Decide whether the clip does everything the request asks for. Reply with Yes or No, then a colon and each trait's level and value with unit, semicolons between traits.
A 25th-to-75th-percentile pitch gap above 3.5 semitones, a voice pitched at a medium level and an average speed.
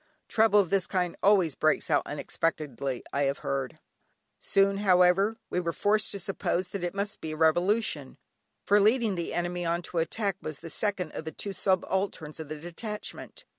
Yes: average, 3.9 semitones; medium, 180 Hz; average, 180 wpm